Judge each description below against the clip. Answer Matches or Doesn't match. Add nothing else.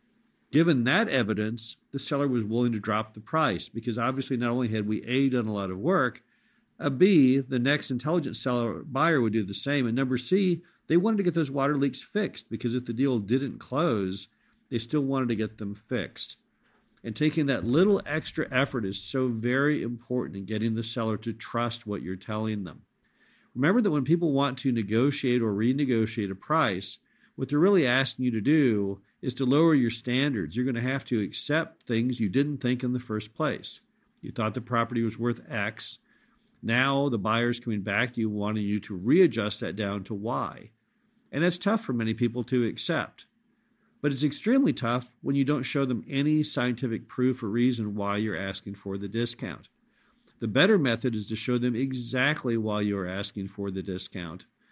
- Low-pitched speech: Matches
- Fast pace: Doesn't match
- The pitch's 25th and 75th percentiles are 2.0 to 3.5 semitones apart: Doesn't match